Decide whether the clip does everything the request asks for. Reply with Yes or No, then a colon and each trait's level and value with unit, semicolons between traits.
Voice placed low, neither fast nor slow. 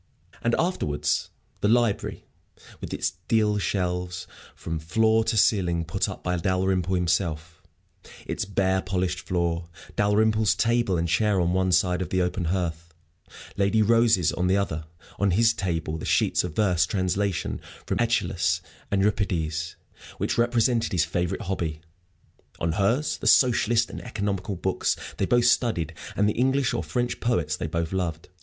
Yes: very low, 95 Hz; average, 155 wpm